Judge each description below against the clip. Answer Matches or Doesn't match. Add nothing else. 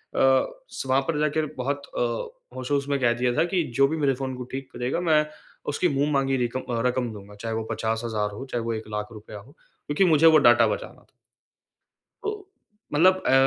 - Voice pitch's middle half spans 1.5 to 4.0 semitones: Doesn't match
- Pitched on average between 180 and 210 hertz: Doesn't match